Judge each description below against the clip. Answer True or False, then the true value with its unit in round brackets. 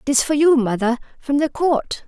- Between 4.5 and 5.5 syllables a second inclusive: True (5.1 syllables/s)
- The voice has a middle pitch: False (275 Hz)